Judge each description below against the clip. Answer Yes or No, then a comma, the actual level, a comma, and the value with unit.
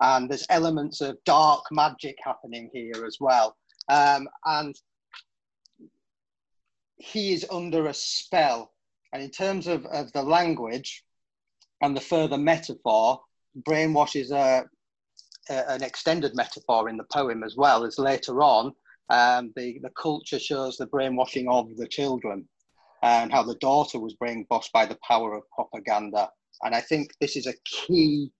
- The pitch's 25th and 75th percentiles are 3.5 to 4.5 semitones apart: Yes, average, 4.1 semitones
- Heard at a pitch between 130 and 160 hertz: Yes, medium, 140 Hz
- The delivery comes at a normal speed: Yes, average, 150 wpm